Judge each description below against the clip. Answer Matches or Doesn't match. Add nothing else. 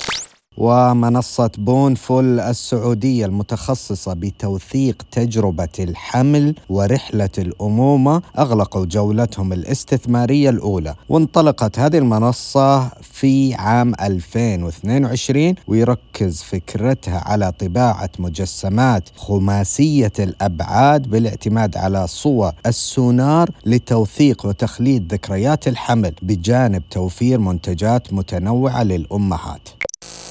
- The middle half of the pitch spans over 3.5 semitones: Matches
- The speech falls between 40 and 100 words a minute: Matches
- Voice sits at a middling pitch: Doesn't match